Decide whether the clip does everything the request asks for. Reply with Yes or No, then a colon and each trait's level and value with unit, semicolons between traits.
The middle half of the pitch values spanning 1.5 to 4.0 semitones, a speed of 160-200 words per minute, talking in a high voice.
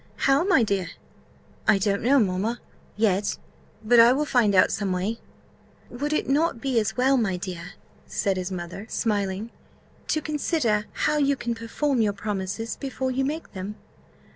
No: average, 5.3 semitones; average, 165 wpm; high, 225 Hz